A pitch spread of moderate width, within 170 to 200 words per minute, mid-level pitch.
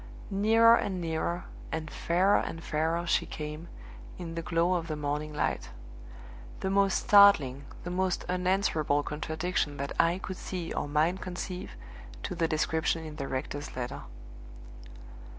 No: average, 3.2 semitones; average, 145 wpm; medium, 165 Hz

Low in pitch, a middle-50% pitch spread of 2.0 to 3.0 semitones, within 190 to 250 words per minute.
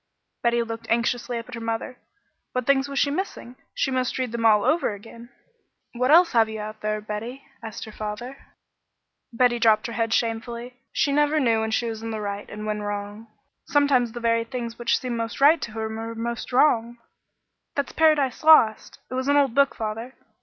No: high, 235 Hz; narrow, 2.6 semitones; average, 200 wpm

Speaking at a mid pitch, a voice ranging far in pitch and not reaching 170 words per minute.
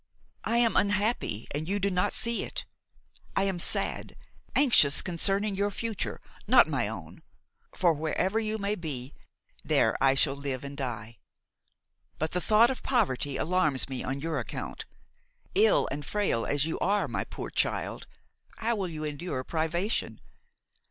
Yes: medium, 175 Hz; wide, 6.7 semitones; average, 155 wpm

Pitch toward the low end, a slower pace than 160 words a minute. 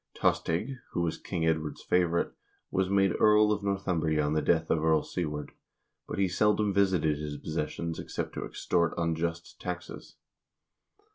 Yes: very low, 85 Hz; average, 150 wpm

